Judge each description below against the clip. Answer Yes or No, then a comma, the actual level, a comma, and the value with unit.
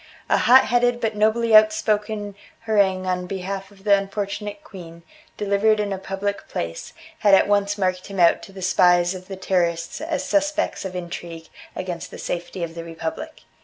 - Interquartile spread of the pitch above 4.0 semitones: No, average, 2.9 semitones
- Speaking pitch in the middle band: No, high, 195 Hz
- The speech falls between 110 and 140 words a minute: No, average, 175 wpm